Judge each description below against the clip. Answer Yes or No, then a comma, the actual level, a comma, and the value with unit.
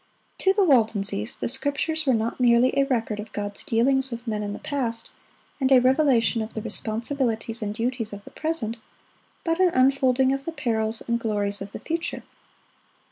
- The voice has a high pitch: Yes, high, 235 Hz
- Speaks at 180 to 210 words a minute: Yes, average, 185 wpm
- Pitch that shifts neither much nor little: Yes, average, 3.7 semitones